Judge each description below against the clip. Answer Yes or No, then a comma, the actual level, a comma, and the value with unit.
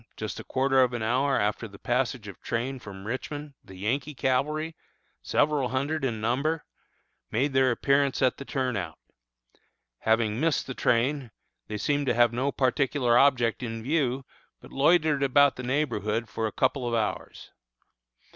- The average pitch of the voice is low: Yes, low, 130 Hz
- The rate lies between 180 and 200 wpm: No, average, 160 wpm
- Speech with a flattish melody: No, average, 3.5 semitones